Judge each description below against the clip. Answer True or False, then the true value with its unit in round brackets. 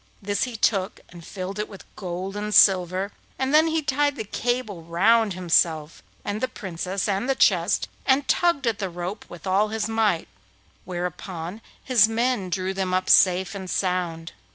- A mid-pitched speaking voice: False (195 Hz)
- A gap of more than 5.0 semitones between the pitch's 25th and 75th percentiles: False (3.7 semitones)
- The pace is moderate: True (175 wpm)